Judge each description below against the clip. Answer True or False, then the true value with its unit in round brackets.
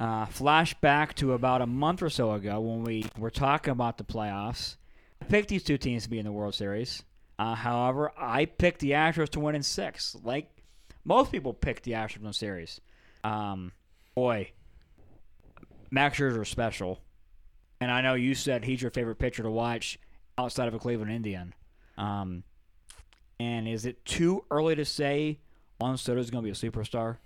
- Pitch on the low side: True (115 Hz)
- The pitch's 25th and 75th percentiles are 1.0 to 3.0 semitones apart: False (4.2 semitones)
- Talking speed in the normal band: True (185 wpm)